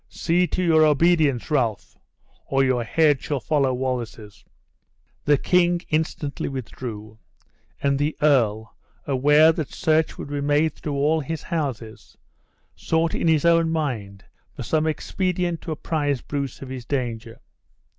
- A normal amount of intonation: Yes, average, 3.9 semitones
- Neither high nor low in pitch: Yes, medium, 145 Hz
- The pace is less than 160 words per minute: Yes, average, 140 wpm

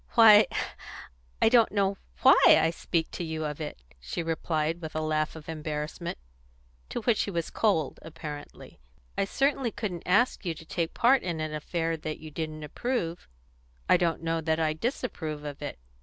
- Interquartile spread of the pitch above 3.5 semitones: Yes, average, 4.0 semitones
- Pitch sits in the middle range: Yes, medium, 165 Hz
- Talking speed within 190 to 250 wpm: No, average, 175 wpm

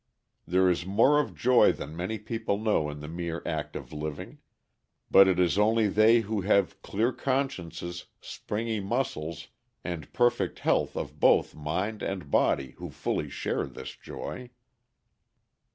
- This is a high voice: No, very low, 95 Hz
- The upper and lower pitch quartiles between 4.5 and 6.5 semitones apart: Yes, average, 4.9 semitones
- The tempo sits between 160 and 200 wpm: No, average, 150 wpm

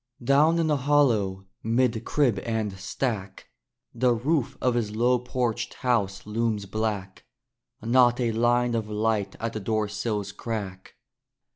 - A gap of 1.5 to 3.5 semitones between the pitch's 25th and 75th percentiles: Yes, average, 2.9 semitones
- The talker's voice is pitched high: No, low, 115 Hz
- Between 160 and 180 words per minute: No, average, 140 wpm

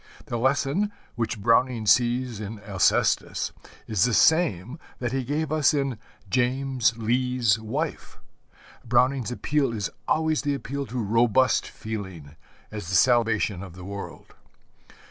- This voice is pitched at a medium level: No, low, 120 Hz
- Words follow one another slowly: Yes, slow, 130 wpm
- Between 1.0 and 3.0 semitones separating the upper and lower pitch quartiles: No, average, 3.9 semitones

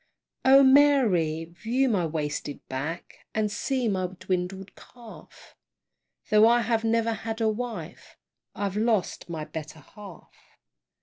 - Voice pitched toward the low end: No, high, 210 Hz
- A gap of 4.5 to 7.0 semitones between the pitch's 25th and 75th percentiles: Yes, average, 4.9 semitones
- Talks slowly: Yes, slow, 125 wpm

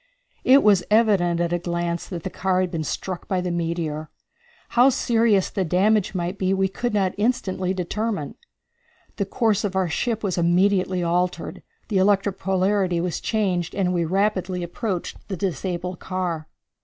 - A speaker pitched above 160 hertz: Yes, medium, 185 Hz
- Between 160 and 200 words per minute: Yes, average, 165 wpm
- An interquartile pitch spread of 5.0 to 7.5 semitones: No, narrow, 2.6 semitones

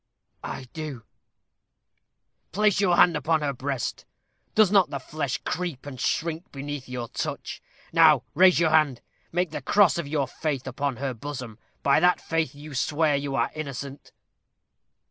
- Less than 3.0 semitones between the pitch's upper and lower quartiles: No, average, 3.3 semitones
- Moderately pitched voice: Yes, medium, 145 Hz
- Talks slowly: No, average, 155 wpm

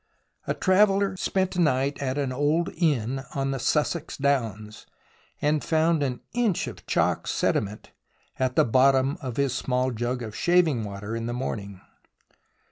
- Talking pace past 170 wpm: No, average, 155 wpm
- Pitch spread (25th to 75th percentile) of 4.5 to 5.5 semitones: Yes, average, 4.9 semitones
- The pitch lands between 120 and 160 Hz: Yes, low, 135 Hz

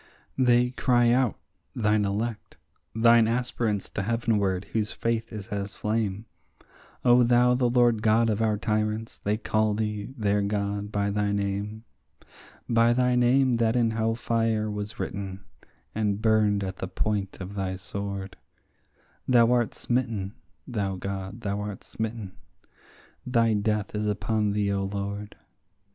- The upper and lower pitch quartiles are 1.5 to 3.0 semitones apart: Yes, narrow, 2.5 semitones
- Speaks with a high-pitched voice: No, low, 105 Hz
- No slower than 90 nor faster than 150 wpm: Yes, average, 145 wpm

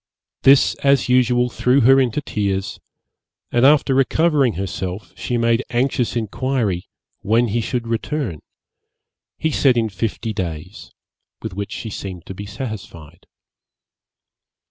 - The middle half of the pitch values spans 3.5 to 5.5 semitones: Yes, average, 4.7 semitones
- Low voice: Yes, low, 115 Hz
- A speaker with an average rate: No, slow, 125 wpm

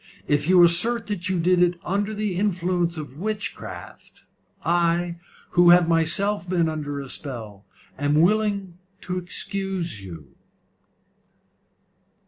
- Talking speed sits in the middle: No, slow, 120 wpm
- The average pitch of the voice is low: No, medium, 175 Hz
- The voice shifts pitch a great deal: No, average, 3.3 semitones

